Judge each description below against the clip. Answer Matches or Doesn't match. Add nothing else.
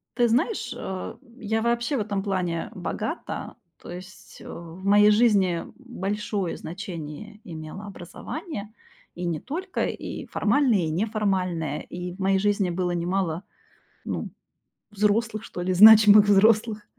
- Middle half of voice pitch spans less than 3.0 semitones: Doesn't match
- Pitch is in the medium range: Doesn't match